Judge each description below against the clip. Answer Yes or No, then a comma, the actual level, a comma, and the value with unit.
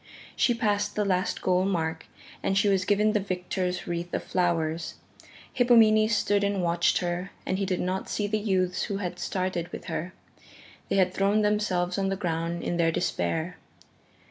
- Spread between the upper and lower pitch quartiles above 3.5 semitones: No, average, 2.7 semitones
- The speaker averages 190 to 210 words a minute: No, average, 175 wpm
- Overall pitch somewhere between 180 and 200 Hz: Yes, medium, 185 Hz